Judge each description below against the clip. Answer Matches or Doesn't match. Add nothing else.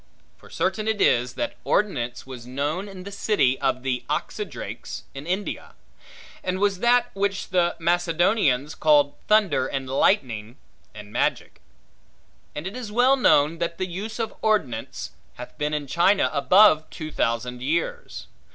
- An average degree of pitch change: Doesn't match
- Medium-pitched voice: Matches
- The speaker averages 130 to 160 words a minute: Matches